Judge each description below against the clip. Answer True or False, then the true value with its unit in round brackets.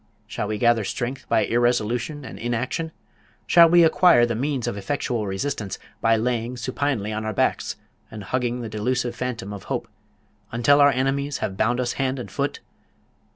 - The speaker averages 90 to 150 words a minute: False (170 wpm)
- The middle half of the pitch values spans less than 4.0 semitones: True (3.4 semitones)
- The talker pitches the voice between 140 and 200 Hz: False (120 Hz)